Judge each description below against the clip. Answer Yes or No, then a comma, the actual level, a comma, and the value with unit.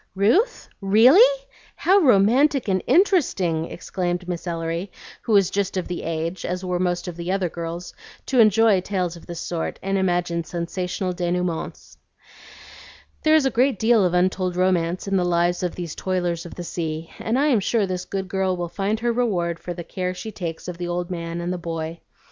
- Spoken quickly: No, average, 195 wpm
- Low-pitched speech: No, medium, 180 Hz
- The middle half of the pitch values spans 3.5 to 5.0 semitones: No, average, 2.8 semitones